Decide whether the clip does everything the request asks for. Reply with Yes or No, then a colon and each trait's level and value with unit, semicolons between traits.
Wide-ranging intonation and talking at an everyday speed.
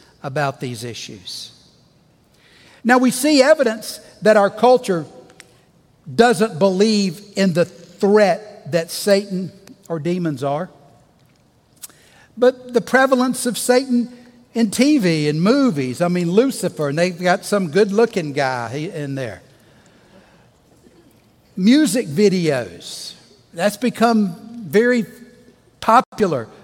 No: wide, 6.0 semitones; slow, 105 wpm